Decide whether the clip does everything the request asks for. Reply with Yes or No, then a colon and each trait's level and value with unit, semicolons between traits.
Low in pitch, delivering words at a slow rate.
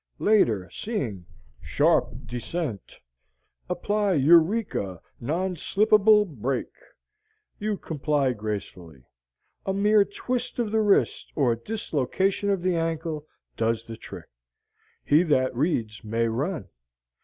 No: medium, 155 Hz; slow, 110 wpm